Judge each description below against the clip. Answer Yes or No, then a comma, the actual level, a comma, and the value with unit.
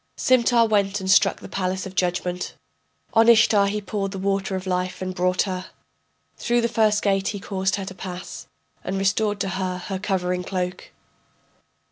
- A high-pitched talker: Yes, high, 195 Hz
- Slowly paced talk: No, average, 175 wpm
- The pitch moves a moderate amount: No, narrow, 2.1 semitones